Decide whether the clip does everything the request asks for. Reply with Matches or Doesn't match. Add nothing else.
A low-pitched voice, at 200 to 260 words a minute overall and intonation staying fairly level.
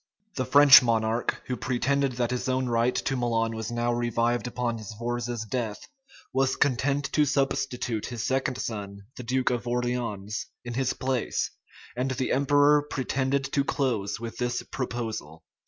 Doesn't match